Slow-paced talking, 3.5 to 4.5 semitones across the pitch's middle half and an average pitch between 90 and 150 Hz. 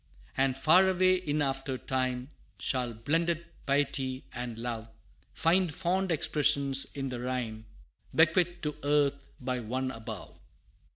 Yes: slow, 125 wpm; average, 4.2 semitones; low, 135 Hz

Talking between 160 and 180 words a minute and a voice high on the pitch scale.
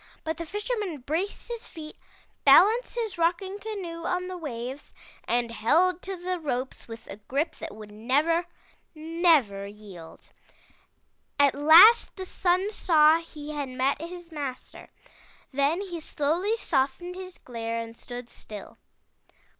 No: average, 140 wpm; very high, 320 Hz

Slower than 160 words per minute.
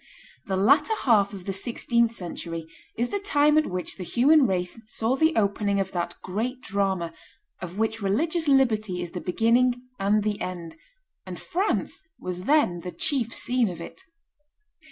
No: average, 165 wpm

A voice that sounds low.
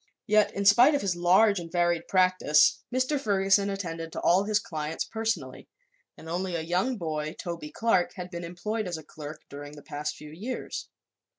No: medium, 180 Hz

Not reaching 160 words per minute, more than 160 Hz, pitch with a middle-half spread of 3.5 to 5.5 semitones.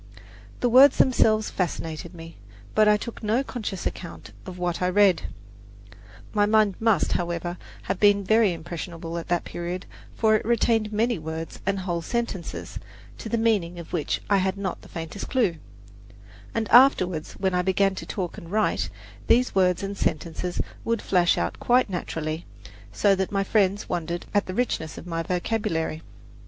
No: average, 170 wpm; high, 190 Hz; average, 3.9 semitones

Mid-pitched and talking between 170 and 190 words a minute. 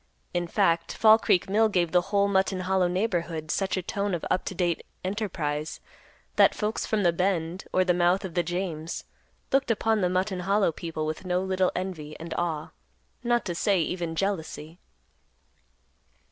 Yes: medium, 180 Hz; average, 175 wpm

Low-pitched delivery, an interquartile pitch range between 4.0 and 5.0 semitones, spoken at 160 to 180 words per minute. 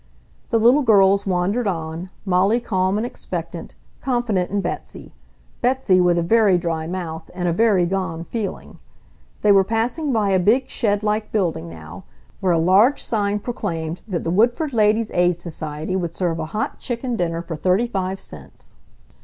No: high, 190 Hz; average, 4.4 semitones; average, 170 wpm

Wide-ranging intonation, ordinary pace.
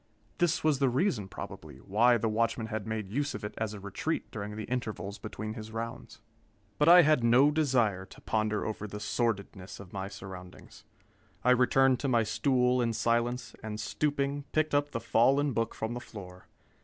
No: average, 3.9 semitones; average, 185 wpm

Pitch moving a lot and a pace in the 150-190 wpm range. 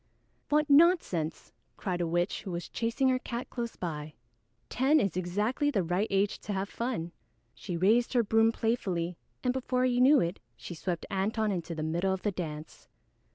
Yes: wide, 5.9 semitones; average, 180 wpm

